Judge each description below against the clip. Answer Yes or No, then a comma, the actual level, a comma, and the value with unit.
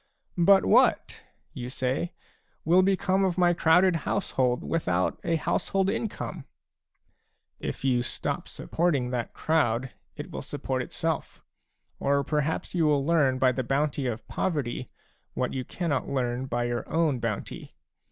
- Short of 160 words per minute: Yes, average, 150 wpm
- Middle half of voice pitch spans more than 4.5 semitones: Yes, average, 5.3 semitones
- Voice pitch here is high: No, medium, 140 Hz